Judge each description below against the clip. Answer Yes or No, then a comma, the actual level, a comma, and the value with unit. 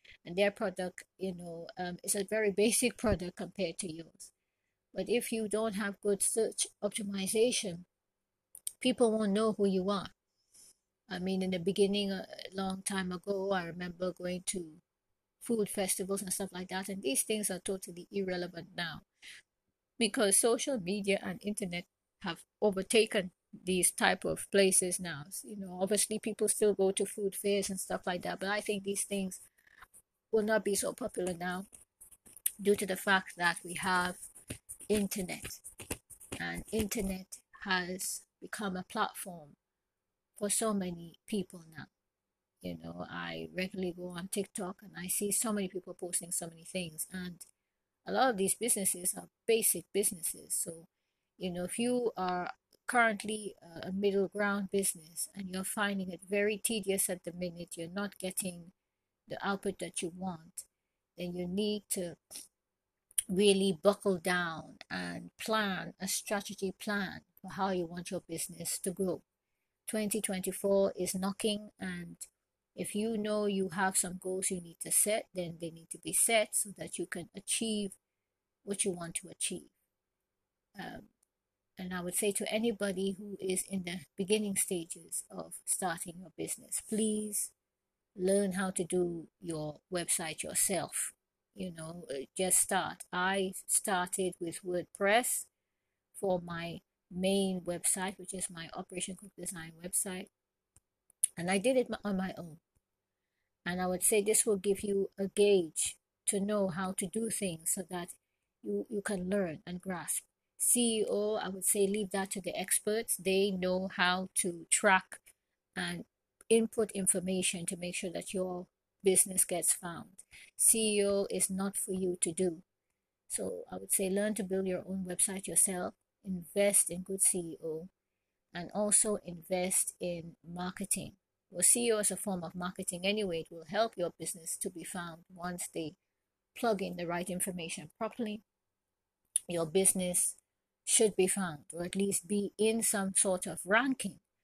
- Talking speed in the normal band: Yes, average, 155 wpm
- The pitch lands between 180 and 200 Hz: Yes, high, 190 Hz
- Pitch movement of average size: No, narrow, 2.3 semitones